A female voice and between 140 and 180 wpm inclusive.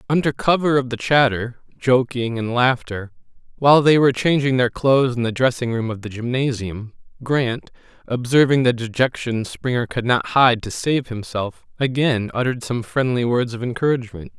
No: male; average, 165 wpm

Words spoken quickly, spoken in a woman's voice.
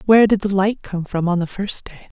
Yes: fast, 275 wpm; female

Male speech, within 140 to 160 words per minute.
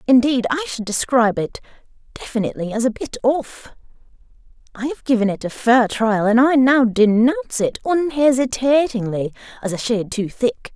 No: female; average, 155 wpm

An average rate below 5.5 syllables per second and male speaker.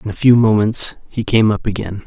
Yes: 5.2 syllables/s; male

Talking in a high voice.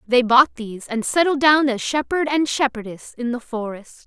Yes: very high, 255 Hz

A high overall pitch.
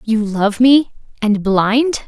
Yes: high, 225 Hz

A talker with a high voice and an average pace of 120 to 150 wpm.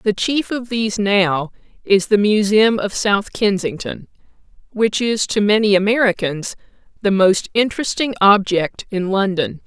Yes: high, 205 Hz; slow, 135 wpm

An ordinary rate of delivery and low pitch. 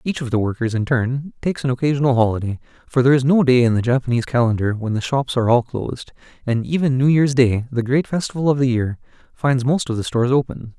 No: fast, 235 wpm; low, 130 Hz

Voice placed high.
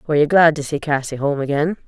No: medium, 150 Hz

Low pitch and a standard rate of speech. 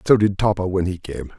No: very low, 95 Hz; fast, 260 wpm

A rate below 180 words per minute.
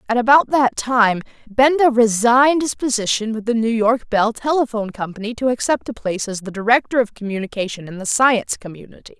No: average, 185 wpm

